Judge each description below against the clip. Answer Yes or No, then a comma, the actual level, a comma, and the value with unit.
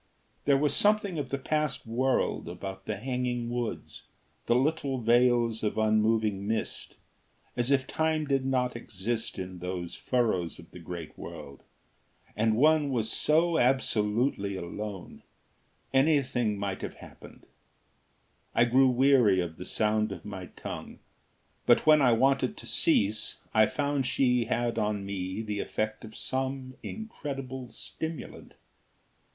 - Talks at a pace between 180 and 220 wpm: No, slow, 135 wpm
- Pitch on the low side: Yes, low, 120 Hz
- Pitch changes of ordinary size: Yes, average, 4.3 semitones